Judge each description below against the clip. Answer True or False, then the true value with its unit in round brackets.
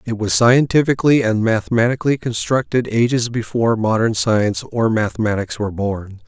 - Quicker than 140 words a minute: False (135 wpm)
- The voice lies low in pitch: True (115 Hz)